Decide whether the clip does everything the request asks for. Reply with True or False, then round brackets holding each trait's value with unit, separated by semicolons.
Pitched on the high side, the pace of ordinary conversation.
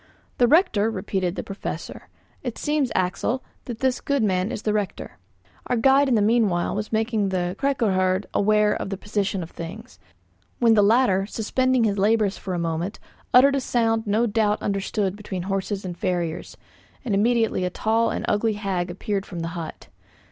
True (210 Hz; 175 wpm)